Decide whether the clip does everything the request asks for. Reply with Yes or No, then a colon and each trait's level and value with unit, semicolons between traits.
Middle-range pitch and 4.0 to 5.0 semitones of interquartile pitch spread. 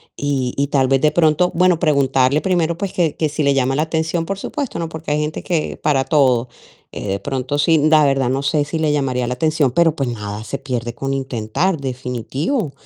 No: medium, 145 Hz; average, 3.5 semitones